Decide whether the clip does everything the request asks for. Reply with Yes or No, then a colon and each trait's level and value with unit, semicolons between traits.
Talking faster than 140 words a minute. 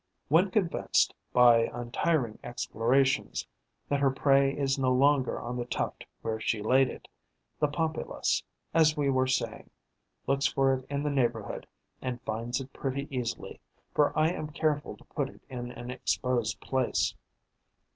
Yes: average, 155 wpm